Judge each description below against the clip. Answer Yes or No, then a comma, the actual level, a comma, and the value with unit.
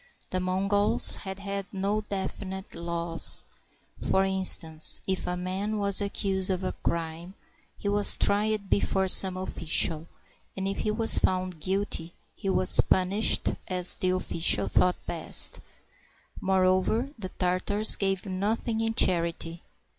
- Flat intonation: Yes, narrow, 1.8 semitones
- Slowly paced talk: Yes, slow, 130 wpm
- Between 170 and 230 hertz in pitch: Yes, high, 190 Hz